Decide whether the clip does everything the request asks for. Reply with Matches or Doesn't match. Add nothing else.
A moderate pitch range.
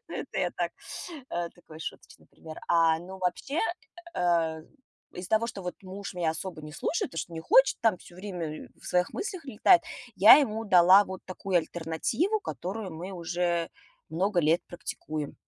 Matches